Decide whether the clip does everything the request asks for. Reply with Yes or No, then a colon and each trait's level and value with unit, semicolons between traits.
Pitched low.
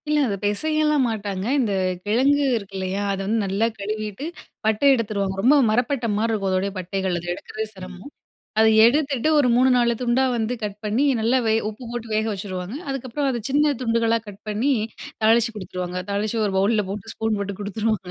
No: high, 220 Hz